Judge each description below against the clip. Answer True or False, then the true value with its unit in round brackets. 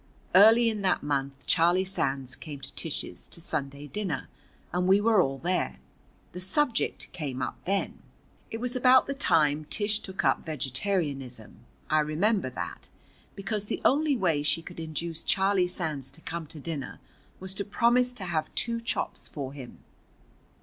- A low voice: False (175 Hz)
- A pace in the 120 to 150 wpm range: False (165 wpm)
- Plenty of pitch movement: True (6.0 semitones)